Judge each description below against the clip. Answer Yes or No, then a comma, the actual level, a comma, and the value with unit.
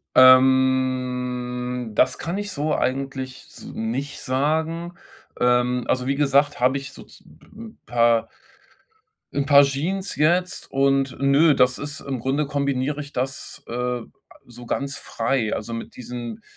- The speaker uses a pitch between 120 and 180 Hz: Yes, low, 135 Hz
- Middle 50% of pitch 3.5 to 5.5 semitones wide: No, narrow, 2.4 semitones